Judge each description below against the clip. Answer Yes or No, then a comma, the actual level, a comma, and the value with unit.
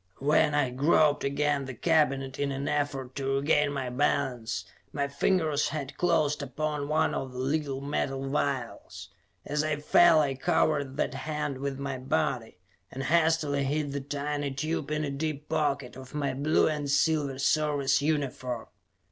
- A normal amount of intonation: No, narrow, 1.8 semitones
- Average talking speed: Yes, average, 165 wpm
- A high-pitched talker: No, medium, 140 Hz